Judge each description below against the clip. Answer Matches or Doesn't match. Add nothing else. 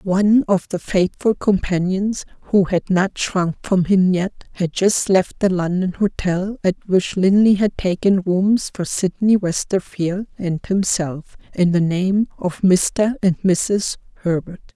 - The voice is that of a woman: Matches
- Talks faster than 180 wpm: Doesn't match